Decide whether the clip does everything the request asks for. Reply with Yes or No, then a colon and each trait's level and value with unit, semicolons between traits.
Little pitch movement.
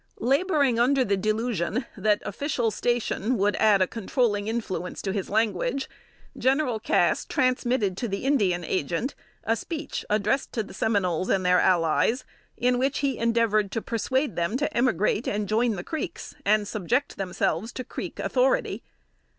No: average, 4.3 semitones